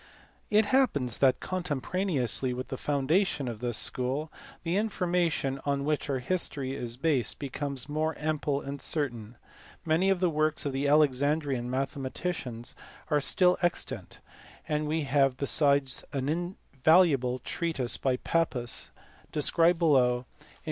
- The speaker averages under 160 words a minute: Yes, average, 140 wpm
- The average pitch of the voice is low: No, medium, 145 Hz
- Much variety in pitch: No, average, 4.0 semitones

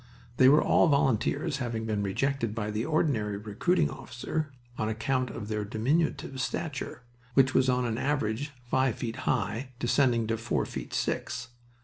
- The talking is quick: No, average, 155 wpm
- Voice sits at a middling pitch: No, low, 125 Hz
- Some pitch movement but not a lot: Yes, average, 3.8 semitones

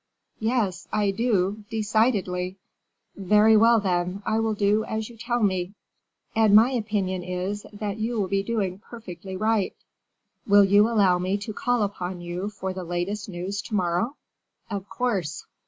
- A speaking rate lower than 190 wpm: Yes, average, 155 wpm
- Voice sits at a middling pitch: No, high, 205 Hz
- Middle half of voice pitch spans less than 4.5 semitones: Yes, average, 2.9 semitones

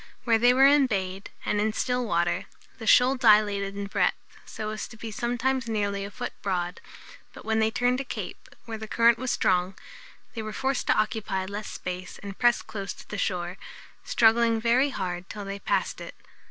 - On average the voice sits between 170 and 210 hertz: No, high, 220 Hz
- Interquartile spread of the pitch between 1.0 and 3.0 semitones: No, average, 3.4 semitones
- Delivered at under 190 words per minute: No, average, 195 wpm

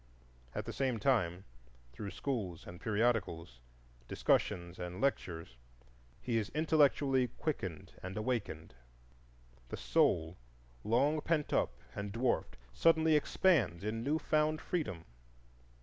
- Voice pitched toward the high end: No, low, 115 Hz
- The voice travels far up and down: Yes, wide, 8.3 semitones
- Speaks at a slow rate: Yes, slow, 115 wpm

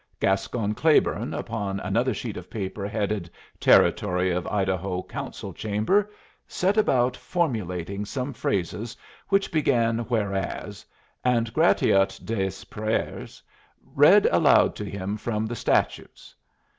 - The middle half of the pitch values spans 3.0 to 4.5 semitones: Yes, average, 3.8 semitones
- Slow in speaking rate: Yes, slow, 115 wpm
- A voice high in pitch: No, low, 105 Hz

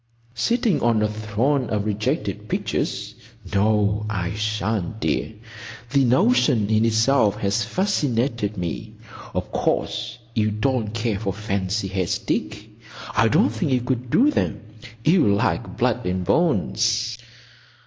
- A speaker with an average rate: No, slow, 130 wpm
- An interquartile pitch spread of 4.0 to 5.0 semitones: No, average, 3.2 semitones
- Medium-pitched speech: No, low, 110 Hz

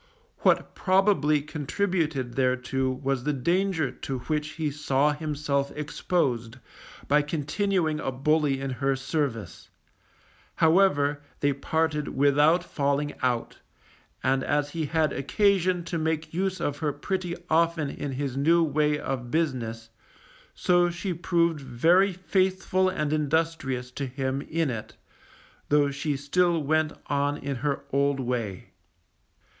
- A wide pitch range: No, average, 3.5 semitones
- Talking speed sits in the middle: No, slow, 130 wpm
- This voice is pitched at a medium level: Yes, medium, 150 Hz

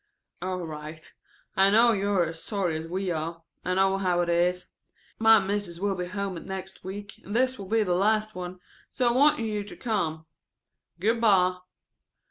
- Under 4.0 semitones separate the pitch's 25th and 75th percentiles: Yes, average, 2.9 semitones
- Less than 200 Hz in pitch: Yes, high, 190 Hz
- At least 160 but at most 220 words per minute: Yes, average, 190 wpm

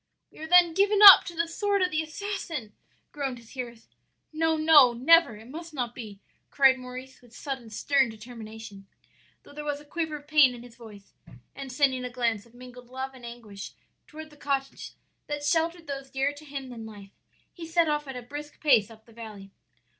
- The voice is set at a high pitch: Yes, very high, 270 Hz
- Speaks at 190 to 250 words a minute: Yes, average, 200 wpm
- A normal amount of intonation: Yes, average, 4.7 semitones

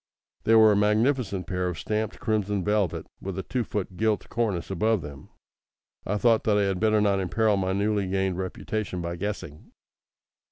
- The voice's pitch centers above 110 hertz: No, low, 105 Hz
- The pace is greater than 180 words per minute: No, average, 175 wpm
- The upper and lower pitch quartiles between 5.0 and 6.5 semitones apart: No, narrow, 2.6 semitones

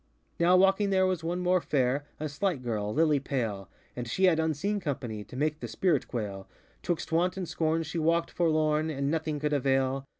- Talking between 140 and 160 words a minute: No, average, 195 wpm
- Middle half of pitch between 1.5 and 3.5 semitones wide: No, average, 4.4 semitones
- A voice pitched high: No, medium, 155 Hz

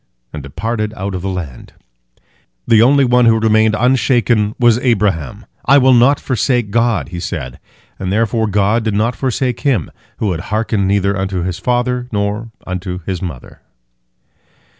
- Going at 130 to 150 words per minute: No, average, 160 wpm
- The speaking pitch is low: Yes, low, 110 Hz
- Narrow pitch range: No, average, 4.0 semitones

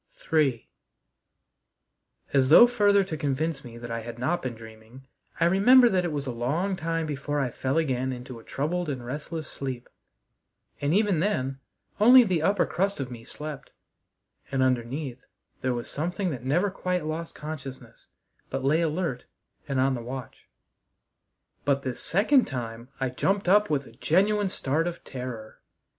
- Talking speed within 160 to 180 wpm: Yes, average, 165 wpm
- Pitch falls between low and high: Yes, medium, 145 Hz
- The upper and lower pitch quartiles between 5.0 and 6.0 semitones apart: Yes, wide, 5.5 semitones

